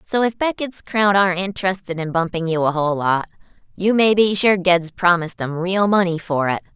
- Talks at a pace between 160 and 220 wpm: Yes, fast, 205 wpm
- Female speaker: Yes, female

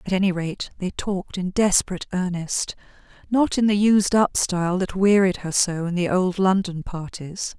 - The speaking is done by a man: No, female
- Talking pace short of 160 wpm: No, average, 175 wpm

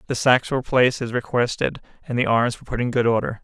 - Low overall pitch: Yes, low, 120 Hz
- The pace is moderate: No, fast, 245 wpm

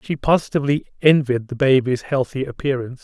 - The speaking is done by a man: Yes, male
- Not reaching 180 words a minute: Yes, average, 140 wpm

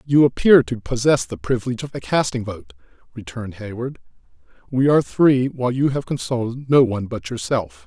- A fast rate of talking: No, average, 175 wpm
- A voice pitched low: Yes, low, 120 Hz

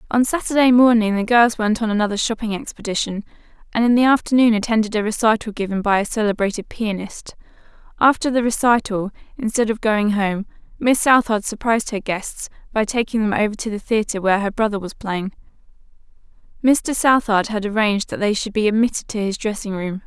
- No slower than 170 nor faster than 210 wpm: Yes, average, 175 wpm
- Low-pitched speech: No, high, 220 Hz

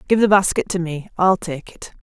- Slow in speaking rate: No, fast, 205 wpm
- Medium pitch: Yes, medium, 180 Hz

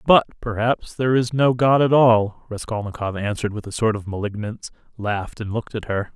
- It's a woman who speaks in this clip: No, male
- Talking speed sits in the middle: Yes, average, 195 wpm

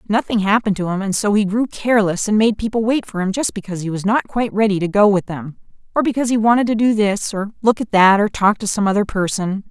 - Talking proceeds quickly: Yes, fast, 265 wpm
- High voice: Yes, high, 210 Hz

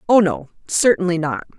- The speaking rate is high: No, average, 150 wpm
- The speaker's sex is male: No, female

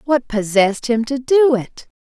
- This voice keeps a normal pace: Yes, average, 175 wpm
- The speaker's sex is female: Yes, female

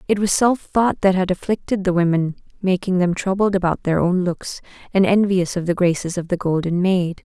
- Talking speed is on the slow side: No, fast, 205 wpm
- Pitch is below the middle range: No, medium, 185 Hz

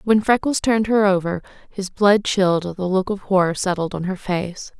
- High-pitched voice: Yes, high, 195 Hz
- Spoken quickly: Yes, fast, 215 wpm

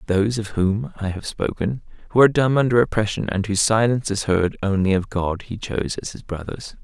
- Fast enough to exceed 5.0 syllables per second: Yes, 5.9 syllables/s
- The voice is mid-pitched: No, low, 105 Hz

